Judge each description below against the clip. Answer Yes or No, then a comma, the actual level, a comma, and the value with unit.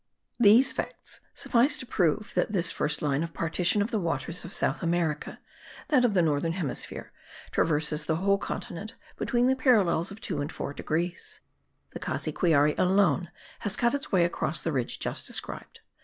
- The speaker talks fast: No, average, 170 wpm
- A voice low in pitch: No, medium, 175 Hz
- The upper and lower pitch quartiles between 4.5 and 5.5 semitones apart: Yes, average, 4.9 semitones